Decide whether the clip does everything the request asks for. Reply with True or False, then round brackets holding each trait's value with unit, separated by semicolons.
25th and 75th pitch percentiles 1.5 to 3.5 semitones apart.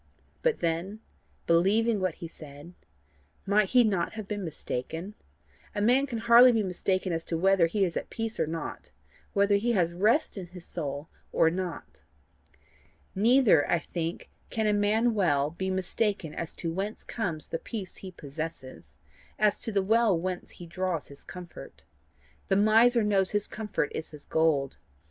False (4.4 semitones)